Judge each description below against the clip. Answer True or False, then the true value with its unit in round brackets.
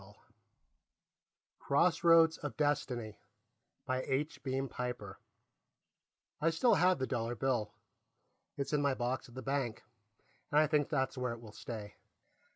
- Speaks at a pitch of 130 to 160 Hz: True (135 Hz)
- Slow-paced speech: True (115 wpm)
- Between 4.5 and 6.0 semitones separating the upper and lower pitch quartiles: False (3.6 semitones)